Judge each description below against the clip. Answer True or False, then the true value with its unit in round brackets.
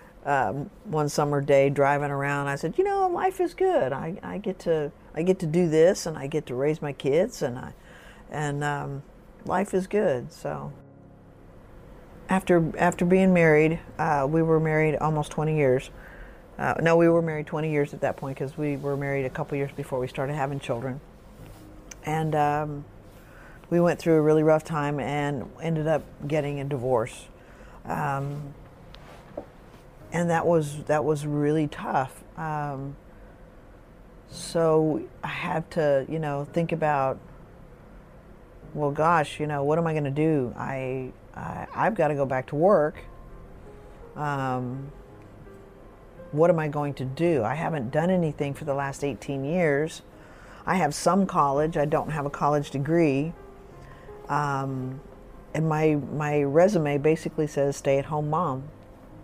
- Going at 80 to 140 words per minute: False (160 wpm)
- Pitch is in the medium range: True (150 Hz)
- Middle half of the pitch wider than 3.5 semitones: False (2.7 semitones)